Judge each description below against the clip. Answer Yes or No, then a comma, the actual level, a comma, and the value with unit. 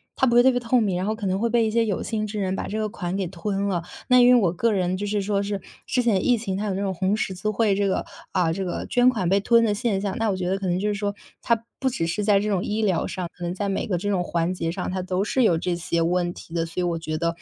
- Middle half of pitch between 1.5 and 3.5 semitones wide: Yes, average, 3.0 semitones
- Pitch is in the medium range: No, high, 195 Hz